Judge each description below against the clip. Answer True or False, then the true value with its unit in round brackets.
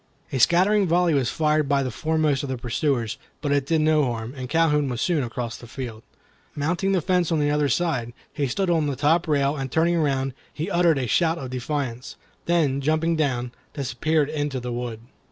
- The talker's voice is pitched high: False (145 Hz)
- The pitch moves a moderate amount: True (3.9 semitones)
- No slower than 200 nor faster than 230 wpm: True (205 wpm)